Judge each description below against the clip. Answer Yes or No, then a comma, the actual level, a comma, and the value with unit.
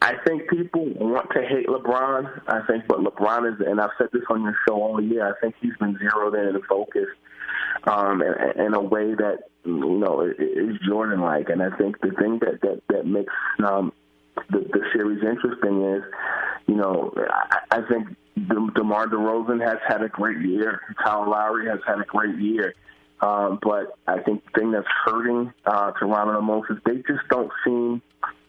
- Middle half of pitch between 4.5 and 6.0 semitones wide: No, narrow, 2.5 semitones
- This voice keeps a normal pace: Yes, average, 190 wpm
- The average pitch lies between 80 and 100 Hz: No, low, 110 Hz